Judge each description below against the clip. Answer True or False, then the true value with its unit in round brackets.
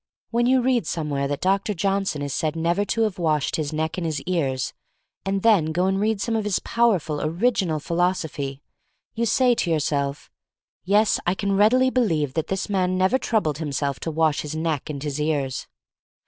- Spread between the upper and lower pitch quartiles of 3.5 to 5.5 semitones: True (5.1 semitones)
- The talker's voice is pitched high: False (170 Hz)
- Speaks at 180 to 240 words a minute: True (190 wpm)